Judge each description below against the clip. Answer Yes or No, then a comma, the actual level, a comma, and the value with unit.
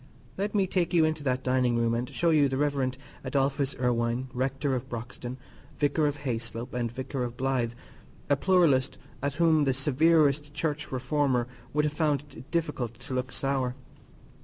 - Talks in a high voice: No, low, 135 Hz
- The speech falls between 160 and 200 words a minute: Yes, average, 170 wpm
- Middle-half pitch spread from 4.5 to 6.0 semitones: No, average, 3.0 semitones